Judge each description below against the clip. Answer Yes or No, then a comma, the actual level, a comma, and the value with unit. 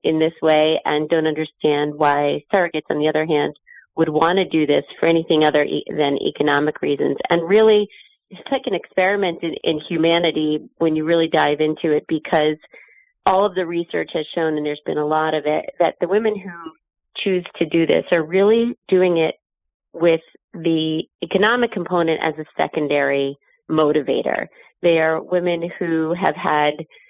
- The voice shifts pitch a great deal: No, average, 2.7 semitones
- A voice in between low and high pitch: Yes, medium, 160 Hz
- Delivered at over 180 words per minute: No, average, 175 wpm